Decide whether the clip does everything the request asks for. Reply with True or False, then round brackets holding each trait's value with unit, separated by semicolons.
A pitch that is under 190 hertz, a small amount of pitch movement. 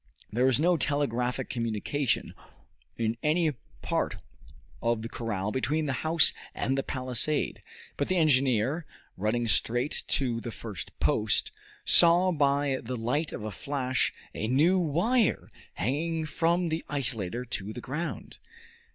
False (135 Hz; 5.0 semitones)